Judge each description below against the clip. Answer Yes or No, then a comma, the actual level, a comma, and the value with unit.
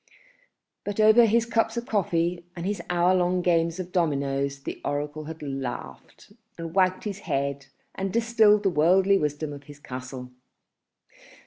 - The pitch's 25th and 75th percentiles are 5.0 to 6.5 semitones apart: Yes, wide, 5.5 semitones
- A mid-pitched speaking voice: Yes, medium, 170 Hz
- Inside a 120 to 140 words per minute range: No, average, 150 wpm